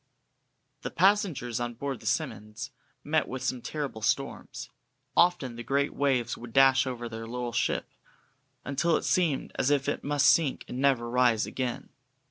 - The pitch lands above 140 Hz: No, low, 130 Hz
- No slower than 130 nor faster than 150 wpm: No, average, 160 wpm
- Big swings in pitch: No, average, 3.0 semitones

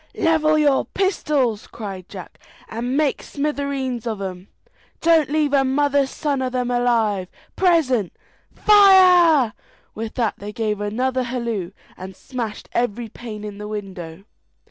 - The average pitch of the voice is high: Yes, high, 245 Hz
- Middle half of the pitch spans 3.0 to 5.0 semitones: No, wide, 5.4 semitones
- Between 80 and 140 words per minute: Yes, slow, 135 wpm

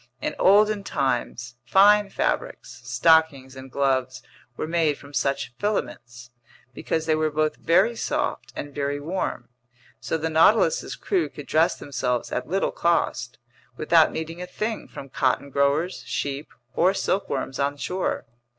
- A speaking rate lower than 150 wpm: Yes, average, 140 wpm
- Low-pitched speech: No, medium, 155 Hz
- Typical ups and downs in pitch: Yes, average, 4.7 semitones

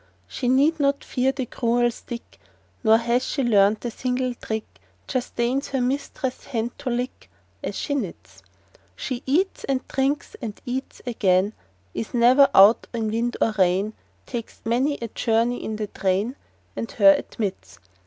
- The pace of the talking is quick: No, average, 160 wpm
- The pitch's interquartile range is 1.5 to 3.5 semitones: Yes, average, 3.0 semitones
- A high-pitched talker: Yes, high, 240 Hz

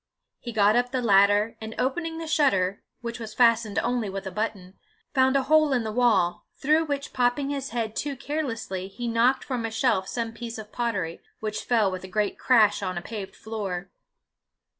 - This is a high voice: Yes, high, 230 Hz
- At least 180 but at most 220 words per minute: Yes, average, 195 wpm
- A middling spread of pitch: Yes, average, 4.2 semitones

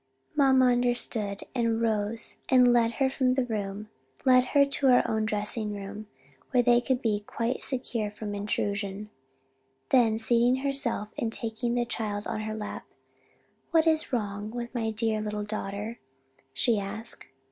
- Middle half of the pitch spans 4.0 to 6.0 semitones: No, average, 2.8 semitones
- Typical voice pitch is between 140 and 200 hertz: No, high, 225 Hz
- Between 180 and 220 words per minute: No, average, 150 wpm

